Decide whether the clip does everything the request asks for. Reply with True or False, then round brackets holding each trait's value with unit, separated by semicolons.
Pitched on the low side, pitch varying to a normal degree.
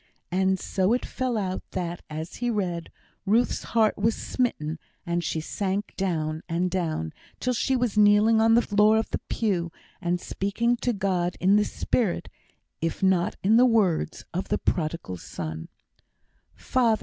False (190 Hz; 4.5 semitones)